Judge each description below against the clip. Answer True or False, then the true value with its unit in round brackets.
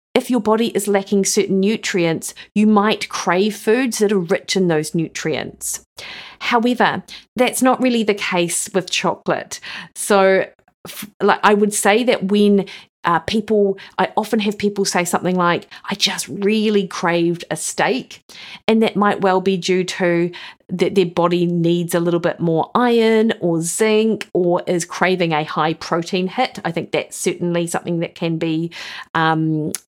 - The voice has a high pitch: True (195 Hz)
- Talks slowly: False (160 wpm)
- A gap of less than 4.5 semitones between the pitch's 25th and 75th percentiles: True (3.4 semitones)